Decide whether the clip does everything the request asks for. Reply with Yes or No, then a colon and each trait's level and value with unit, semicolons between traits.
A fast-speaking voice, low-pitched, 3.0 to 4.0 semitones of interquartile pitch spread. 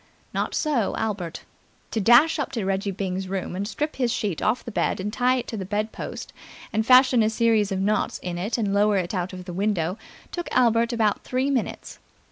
No: fast, 215 wpm; high, 215 Hz; average, 3.7 semitones